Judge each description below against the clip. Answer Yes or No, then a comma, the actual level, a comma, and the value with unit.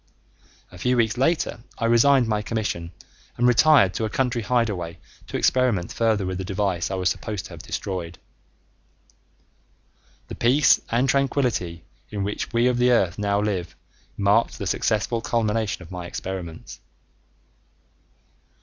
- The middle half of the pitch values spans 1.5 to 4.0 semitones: No, average, 4.6 semitones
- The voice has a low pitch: Yes, low, 105 Hz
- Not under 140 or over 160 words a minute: Yes, average, 145 wpm